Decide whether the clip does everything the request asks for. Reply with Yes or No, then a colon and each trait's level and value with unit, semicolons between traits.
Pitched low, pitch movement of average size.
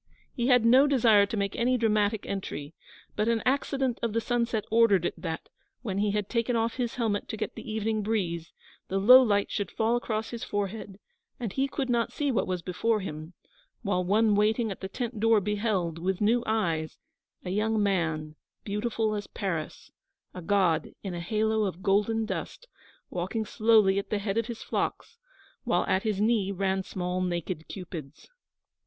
No: high, 210 Hz; average, 3.1 semitones